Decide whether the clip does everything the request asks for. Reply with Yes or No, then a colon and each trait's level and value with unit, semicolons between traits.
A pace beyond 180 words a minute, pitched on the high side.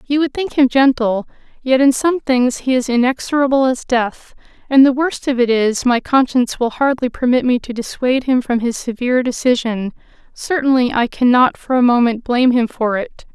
Yes: average, 195 wpm; very high, 250 Hz